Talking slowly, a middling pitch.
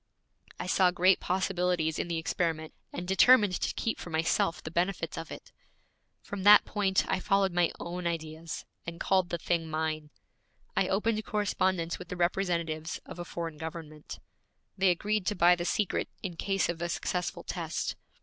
No: average, 170 wpm; medium, 175 Hz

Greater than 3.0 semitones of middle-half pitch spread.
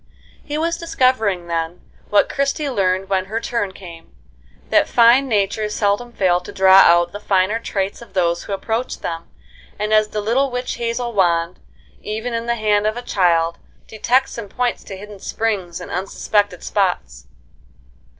Yes: average, 4.1 semitones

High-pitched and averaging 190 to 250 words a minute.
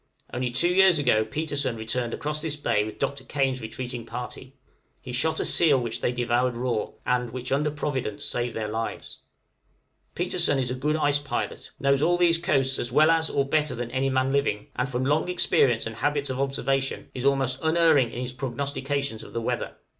No: low, 135 Hz; average, 195 wpm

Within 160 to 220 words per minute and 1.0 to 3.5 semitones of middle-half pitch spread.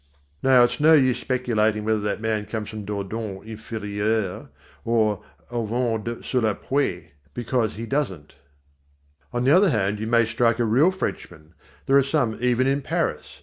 Yes: average, 165 wpm; average, 3.0 semitones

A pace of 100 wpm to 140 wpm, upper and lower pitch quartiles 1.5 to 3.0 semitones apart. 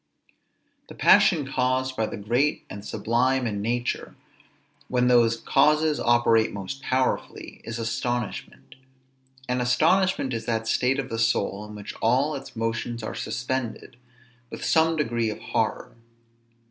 Yes: slow, 135 wpm; average, 2.7 semitones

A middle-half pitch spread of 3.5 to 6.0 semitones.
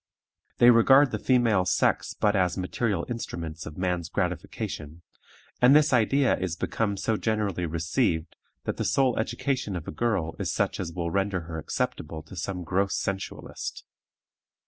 Yes: wide, 5.4 semitones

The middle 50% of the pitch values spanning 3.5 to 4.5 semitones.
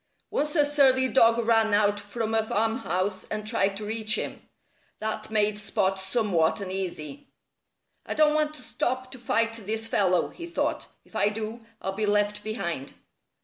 No: average, 2.8 semitones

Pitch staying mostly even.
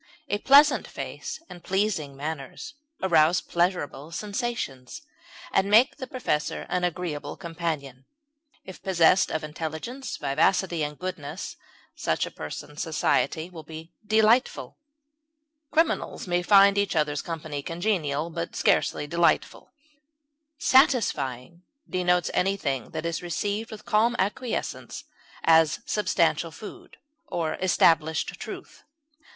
No: average, 4.5 semitones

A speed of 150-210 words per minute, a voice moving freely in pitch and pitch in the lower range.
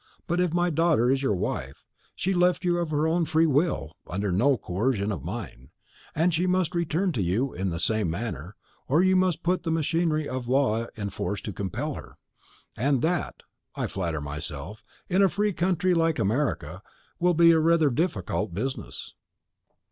No: average, 185 wpm; wide, 9.0 semitones; medium, 145 Hz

